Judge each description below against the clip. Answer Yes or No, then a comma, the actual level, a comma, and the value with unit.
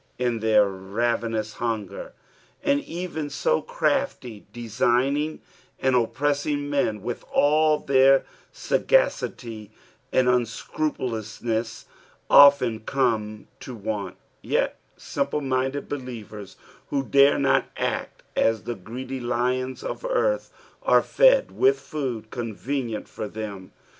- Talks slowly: Yes, slow, 110 wpm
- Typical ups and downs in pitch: Yes, average, 4.5 semitones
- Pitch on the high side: No, low, 125 Hz